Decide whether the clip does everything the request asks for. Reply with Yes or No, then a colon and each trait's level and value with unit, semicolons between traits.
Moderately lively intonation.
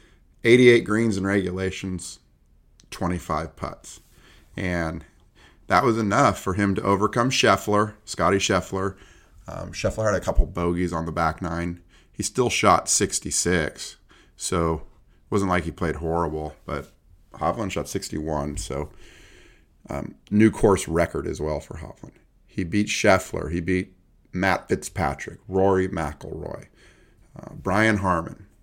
Yes: average, 3.5 semitones